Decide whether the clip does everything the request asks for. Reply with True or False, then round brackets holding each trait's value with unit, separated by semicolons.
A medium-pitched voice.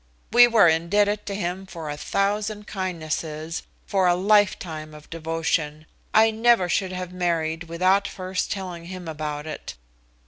True (180 Hz)